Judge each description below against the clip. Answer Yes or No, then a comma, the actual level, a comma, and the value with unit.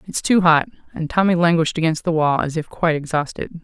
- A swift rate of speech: Yes, fast, 215 wpm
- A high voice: No, medium, 165 Hz